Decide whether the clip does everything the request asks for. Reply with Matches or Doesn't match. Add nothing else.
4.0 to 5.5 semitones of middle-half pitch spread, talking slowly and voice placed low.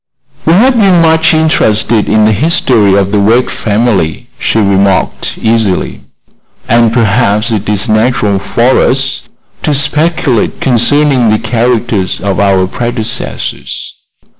Matches